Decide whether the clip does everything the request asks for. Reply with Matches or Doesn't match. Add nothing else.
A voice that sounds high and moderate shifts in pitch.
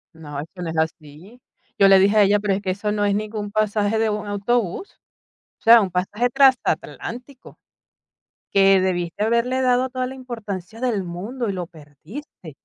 Matches